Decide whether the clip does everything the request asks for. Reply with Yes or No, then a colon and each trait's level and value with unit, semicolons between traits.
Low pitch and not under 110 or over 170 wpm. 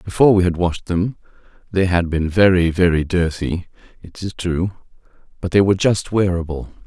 Yes: very low, 90 Hz; average, 165 wpm